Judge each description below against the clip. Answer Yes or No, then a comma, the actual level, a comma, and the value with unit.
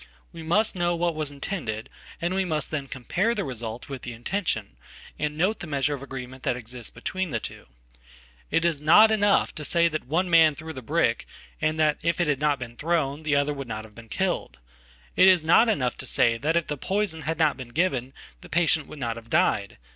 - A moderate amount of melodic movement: Yes, average, 4.8 semitones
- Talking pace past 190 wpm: Yes, fast, 205 wpm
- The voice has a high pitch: No, medium, 150 Hz